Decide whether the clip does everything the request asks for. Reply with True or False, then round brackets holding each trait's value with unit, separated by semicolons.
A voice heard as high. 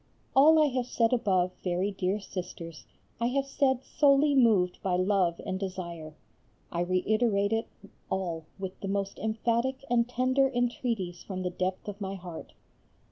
True (200 Hz)